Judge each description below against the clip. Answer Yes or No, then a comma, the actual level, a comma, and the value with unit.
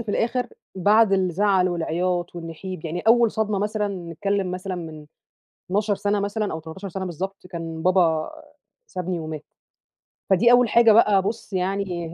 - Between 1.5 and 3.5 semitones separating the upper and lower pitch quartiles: Yes, average, 3.1 semitones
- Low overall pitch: No, high, 190 Hz